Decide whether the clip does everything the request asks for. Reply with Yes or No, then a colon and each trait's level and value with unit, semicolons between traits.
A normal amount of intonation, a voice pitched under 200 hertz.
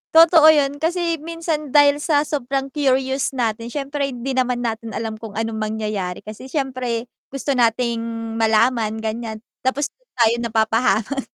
No: average, 4.2 semitones; very high, 255 Hz